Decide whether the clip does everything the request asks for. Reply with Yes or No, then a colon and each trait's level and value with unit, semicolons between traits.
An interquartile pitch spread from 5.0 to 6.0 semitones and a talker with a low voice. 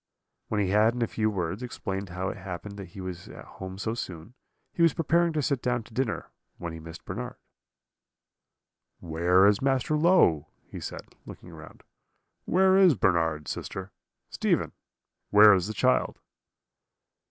Yes: wide, 5.6 semitones; low, 100 Hz